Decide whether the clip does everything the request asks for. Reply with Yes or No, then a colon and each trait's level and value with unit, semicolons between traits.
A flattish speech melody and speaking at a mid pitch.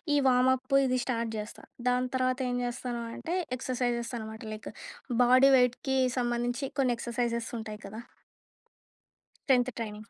No: narrow, 1.7 semitones; high, 245 Hz